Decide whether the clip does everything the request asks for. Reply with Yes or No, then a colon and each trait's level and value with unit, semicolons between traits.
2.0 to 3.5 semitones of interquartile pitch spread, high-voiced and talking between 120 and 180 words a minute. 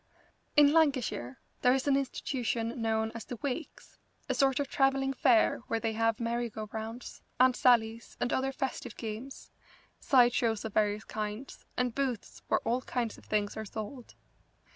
Yes: average, 3.1 semitones; high, 240 Hz; average, 165 wpm